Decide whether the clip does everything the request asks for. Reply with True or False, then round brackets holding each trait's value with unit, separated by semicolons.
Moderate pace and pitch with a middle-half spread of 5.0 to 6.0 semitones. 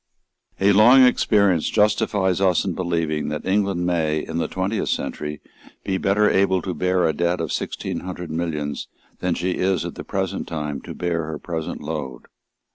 False (175 wpm; 3.4 semitones)